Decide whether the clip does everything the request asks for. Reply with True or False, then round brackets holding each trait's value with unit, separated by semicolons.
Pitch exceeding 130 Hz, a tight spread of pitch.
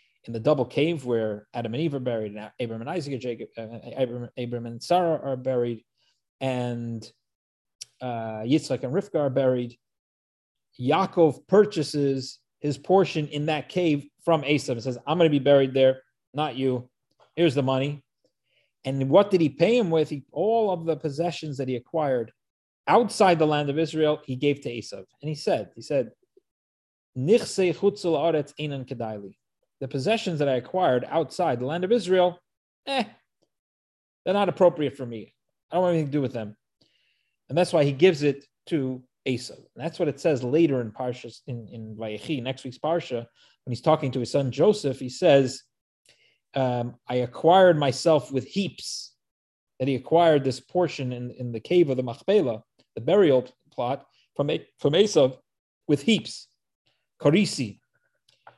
False (140 Hz; 4.9 semitones)